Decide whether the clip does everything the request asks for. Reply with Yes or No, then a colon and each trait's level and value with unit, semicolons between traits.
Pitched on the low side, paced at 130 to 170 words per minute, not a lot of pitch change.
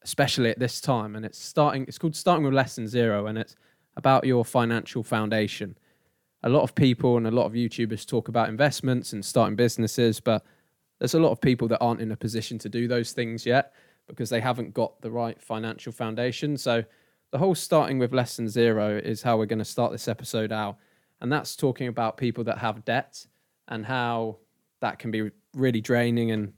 No: low, 120 Hz; fast, 205 wpm; narrow, 2.2 semitones